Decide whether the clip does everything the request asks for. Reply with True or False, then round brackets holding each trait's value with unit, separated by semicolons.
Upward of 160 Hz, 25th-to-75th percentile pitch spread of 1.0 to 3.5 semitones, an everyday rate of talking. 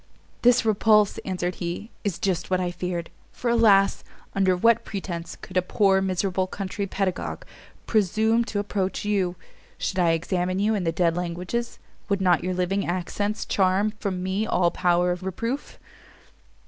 True (190 Hz; 2.5 semitones; 160 wpm)